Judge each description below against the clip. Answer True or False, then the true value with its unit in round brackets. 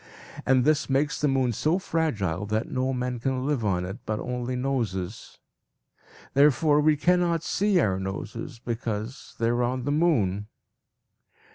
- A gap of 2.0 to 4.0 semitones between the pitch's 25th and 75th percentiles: False (5.4 semitones)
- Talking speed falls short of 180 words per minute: True (150 wpm)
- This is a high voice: False (125 Hz)